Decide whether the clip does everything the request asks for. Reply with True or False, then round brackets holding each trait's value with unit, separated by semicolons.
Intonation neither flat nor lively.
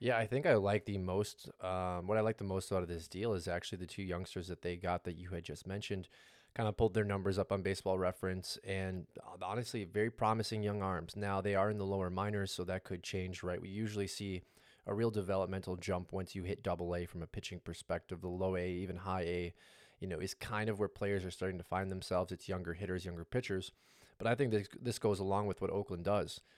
False (2.2 semitones)